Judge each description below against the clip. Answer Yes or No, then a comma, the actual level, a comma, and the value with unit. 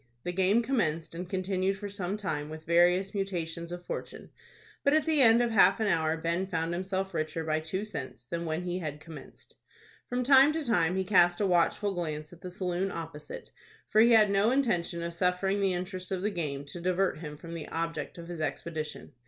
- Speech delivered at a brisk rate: Yes, fast, 210 wpm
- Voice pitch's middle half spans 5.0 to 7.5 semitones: No, average, 3.2 semitones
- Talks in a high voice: No, medium, 180 Hz